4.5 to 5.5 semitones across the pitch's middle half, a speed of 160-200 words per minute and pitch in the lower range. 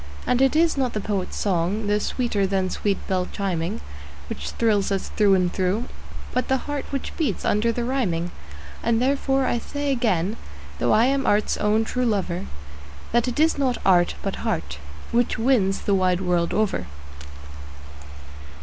No: average, 5.0 semitones; average, 165 wpm; high, 210 Hz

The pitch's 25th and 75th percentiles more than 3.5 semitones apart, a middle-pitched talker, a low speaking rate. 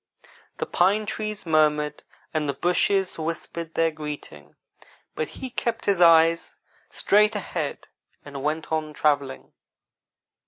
Yes: average, 4.0 semitones; medium, 160 Hz; slow, 120 wpm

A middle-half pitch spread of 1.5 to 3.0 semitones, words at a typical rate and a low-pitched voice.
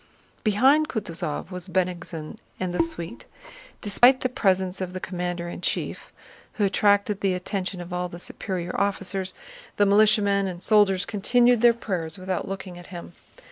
No: narrow, 2.6 semitones; average, 155 wpm; high, 190 Hz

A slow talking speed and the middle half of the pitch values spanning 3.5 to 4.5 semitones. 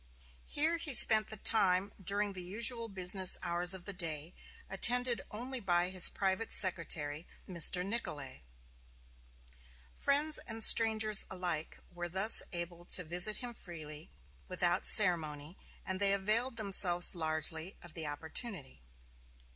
Yes: slow, 130 wpm; average, 4.1 semitones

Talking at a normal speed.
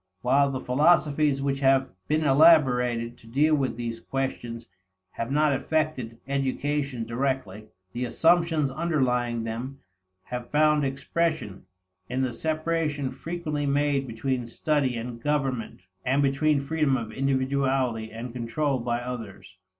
No: slow, 125 wpm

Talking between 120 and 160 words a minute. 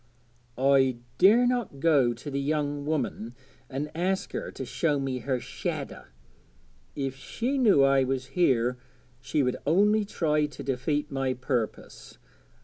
Yes: average, 140 wpm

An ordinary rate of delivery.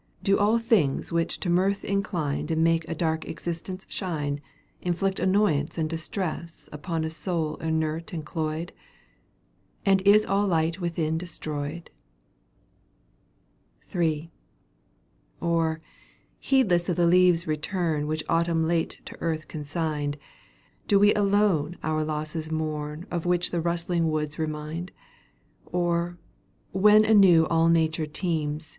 No: slow, 130 wpm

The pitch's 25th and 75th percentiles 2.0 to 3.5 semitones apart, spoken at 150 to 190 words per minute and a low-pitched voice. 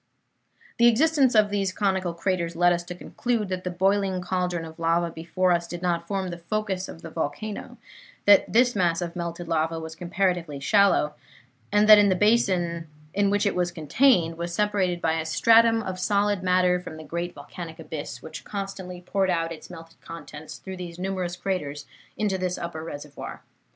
No: average, 3.0 semitones; average, 180 wpm; medium, 180 Hz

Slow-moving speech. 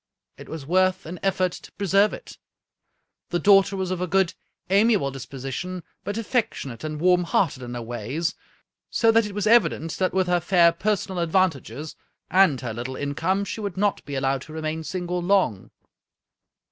No: average, 170 wpm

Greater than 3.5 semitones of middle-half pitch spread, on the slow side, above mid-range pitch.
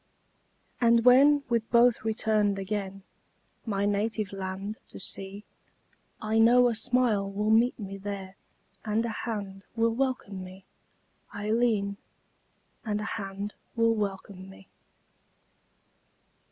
No: narrow, 2.6 semitones; slow, 115 wpm; high, 210 Hz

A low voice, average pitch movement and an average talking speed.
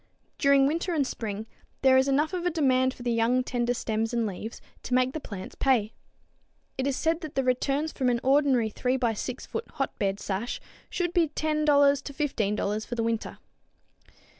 No: very high, 260 Hz; average, 3.9 semitones; average, 190 wpm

